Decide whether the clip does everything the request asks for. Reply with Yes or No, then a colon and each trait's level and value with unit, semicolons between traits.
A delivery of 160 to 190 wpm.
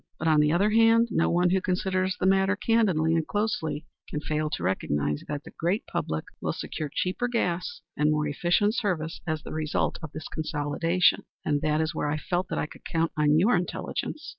No: fast, 205 wpm